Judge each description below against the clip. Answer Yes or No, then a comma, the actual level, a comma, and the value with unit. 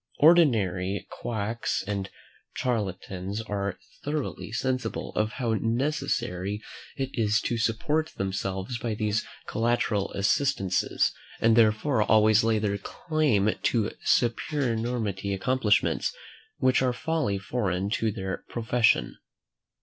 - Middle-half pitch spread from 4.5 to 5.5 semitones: No, average, 3.8 semitones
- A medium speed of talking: No, slow, 105 wpm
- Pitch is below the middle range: Yes, low, 110 Hz